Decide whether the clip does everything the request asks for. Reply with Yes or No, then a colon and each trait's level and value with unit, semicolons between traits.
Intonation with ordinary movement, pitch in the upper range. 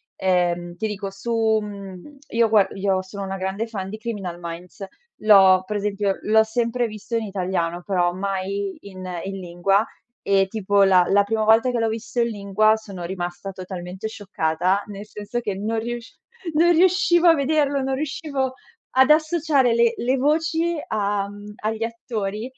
Yes: average, 3.5 semitones; high, 210 Hz